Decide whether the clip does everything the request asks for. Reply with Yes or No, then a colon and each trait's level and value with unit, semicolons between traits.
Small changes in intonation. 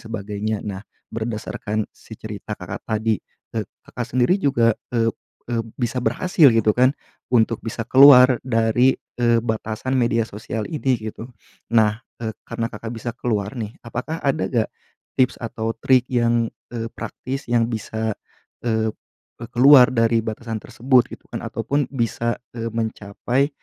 Yes: narrow, 2.1 semitones